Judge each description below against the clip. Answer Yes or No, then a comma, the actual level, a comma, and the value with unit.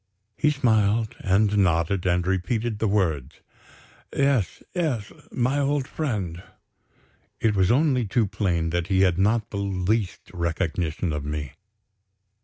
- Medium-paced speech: No, slow, 130 wpm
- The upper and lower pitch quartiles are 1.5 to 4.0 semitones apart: No, average, 4.8 semitones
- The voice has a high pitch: No, low, 100 Hz